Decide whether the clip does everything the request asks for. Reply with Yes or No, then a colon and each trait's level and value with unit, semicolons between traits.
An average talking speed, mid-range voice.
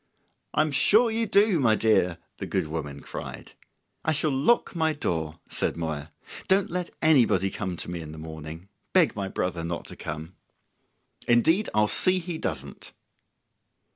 No: average, 160 wpm; low, 110 Hz